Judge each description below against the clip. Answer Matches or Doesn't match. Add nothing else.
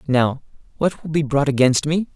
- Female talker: Doesn't match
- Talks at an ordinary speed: Matches